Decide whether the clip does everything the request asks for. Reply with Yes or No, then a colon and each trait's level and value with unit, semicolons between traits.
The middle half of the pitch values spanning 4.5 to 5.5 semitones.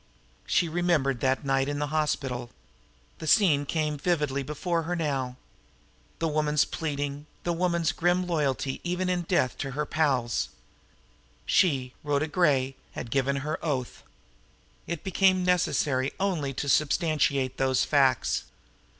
No: average, 4.0 semitones